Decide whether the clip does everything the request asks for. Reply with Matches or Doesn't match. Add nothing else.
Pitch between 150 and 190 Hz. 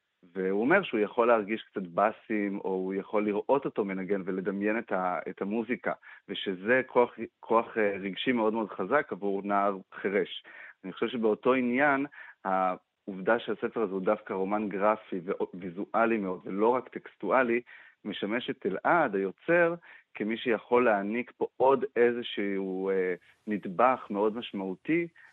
Doesn't match